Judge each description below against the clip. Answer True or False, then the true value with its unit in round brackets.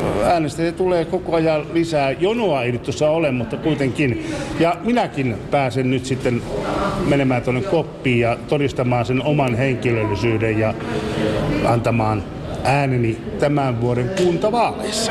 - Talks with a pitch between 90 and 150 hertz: True (135 Hz)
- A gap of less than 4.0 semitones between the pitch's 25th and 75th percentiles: False (4.7 semitones)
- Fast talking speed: False (125 wpm)